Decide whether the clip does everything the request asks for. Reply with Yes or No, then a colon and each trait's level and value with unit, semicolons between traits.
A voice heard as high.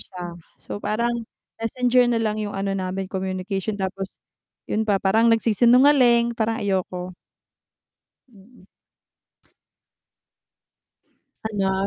Yes: high, 210 Hz